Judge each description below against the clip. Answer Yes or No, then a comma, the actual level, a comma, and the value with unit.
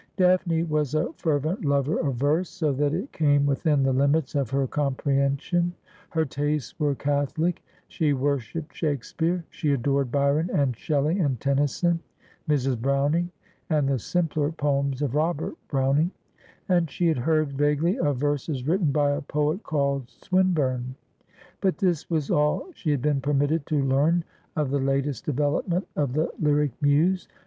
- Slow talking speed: No, average, 155 wpm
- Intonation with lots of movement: No, narrow, 2.6 semitones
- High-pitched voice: No, medium, 145 Hz